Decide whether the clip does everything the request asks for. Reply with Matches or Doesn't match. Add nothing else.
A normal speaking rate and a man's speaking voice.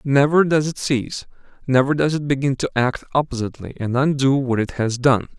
Matches